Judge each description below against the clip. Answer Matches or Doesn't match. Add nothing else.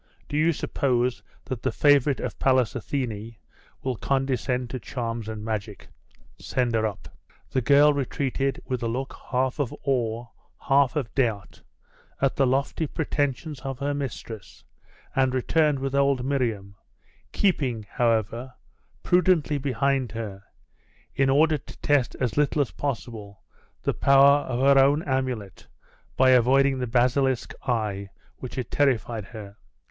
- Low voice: Matches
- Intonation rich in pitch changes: Doesn't match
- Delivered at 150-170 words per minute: Doesn't match